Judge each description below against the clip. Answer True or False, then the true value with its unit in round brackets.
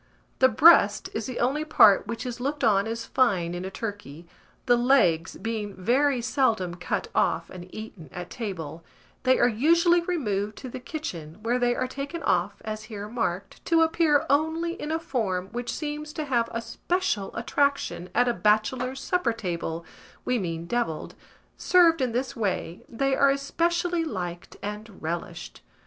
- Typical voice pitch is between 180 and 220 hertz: False (235 Hz)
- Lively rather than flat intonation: True (6.3 semitones)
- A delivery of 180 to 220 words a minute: False (165 wpm)